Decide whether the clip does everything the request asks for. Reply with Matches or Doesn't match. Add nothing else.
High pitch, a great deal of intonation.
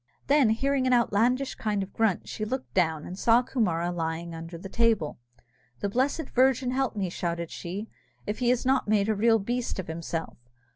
Matches